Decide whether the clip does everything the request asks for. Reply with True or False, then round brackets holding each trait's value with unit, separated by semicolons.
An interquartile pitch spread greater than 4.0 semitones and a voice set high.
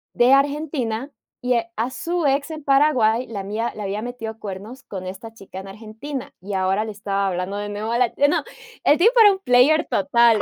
True (5.0 semitones; 230 Hz)